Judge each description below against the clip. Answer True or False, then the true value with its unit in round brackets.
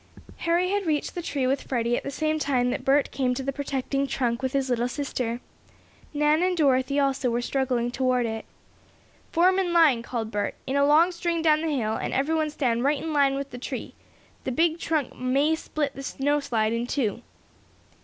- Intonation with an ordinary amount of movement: True (3.7 semitones)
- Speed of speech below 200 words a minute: False (205 wpm)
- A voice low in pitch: False (275 Hz)